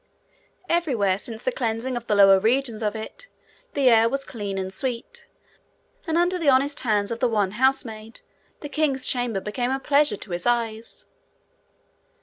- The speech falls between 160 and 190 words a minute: Yes, average, 165 wpm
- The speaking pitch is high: Yes, high, 235 Hz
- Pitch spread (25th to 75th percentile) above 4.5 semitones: No, average, 4.2 semitones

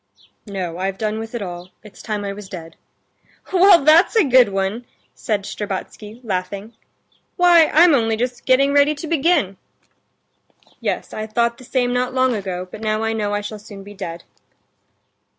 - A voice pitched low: No, high, 220 Hz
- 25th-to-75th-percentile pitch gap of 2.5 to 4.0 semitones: No, average, 4.5 semitones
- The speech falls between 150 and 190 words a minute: Yes, average, 170 wpm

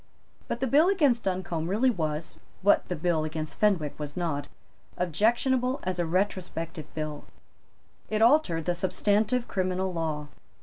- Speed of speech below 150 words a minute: Yes, average, 140 wpm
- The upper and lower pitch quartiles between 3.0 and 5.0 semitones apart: No, wide, 5.4 semitones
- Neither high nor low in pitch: Yes, medium, 180 Hz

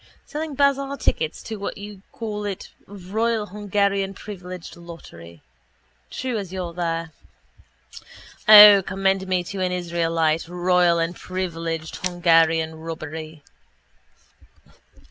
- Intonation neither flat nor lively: Yes, average, 3.5 semitones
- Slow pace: Yes, slow, 110 wpm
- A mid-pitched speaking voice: Yes, medium, 180 Hz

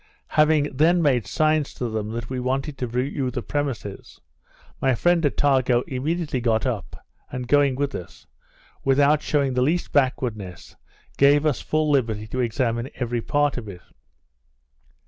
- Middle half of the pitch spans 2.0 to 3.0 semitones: No, average, 3.5 semitones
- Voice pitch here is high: No, low, 130 Hz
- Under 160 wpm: Yes, average, 150 wpm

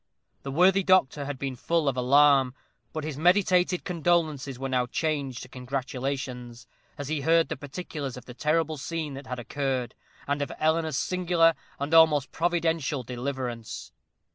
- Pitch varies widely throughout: No, average, 3.8 semitones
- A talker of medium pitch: Yes, medium, 145 Hz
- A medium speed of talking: Yes, average, 155 wpm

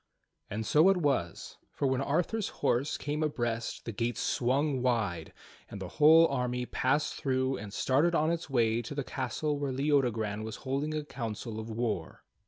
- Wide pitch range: No, average, 4.5 semitones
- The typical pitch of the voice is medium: No, low, 130 Hz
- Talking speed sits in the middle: Yes, average, 175 wpm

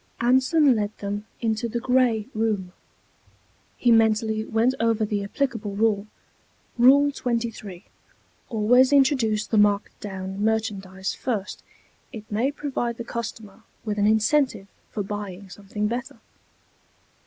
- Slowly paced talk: Yes, slow, 120 wpm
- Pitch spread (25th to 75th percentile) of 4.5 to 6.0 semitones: No, average, 2.9 semitones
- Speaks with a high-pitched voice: Yes, high, 220 Hz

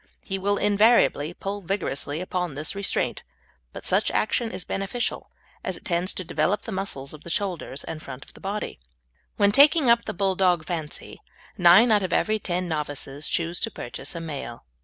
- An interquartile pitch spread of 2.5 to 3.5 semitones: No, average, 4.2 semitones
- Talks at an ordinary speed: Yes, average, 180 wpm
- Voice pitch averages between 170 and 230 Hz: Yes, medium, 185 Hz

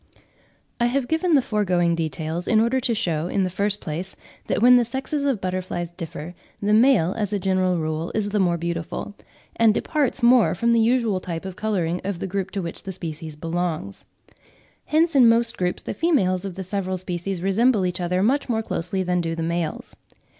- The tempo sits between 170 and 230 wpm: Yes, average, 200 wpm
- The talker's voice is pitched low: No, high, 190 Hz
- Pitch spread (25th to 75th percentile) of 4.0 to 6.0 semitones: Yes, average, 4.9 semitones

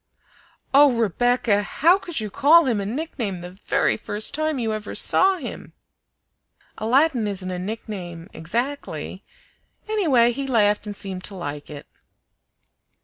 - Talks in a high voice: Yes, high, 225 Hz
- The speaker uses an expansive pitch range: Yes, wide, 5.9 semitones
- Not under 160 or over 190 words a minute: No, average, 140 wpm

